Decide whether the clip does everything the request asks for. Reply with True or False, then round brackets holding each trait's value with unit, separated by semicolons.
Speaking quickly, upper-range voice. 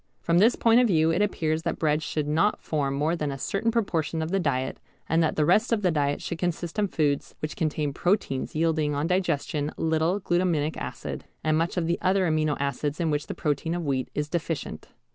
False (220 wpm; 160 Hz)